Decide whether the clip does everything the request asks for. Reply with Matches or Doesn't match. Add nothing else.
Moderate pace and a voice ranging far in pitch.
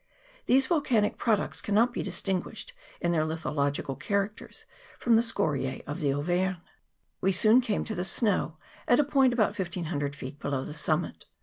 Matches